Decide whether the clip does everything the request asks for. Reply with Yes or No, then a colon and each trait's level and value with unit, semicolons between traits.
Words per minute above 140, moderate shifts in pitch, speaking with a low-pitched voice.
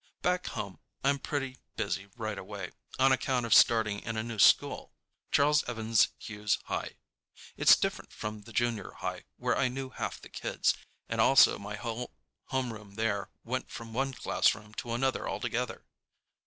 Yes: average, 160 wpm; average, 3.6 semitones; low, 115 Hz